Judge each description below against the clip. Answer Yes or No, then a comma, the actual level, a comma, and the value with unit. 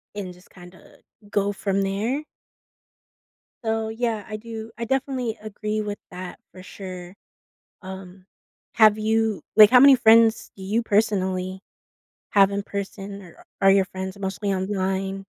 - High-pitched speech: Yes, high, 200 Hz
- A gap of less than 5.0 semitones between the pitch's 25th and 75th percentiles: Yes, average, 2.7 semitones